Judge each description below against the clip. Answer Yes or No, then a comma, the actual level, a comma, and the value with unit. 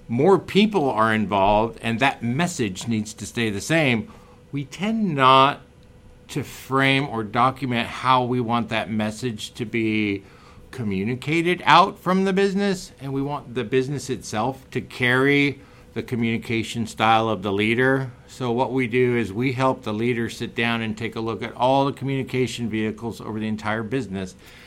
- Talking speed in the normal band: Yes, average, 170 wpm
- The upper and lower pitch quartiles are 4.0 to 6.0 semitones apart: No, average, 3.2 semitones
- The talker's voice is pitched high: No, low, 120 Hz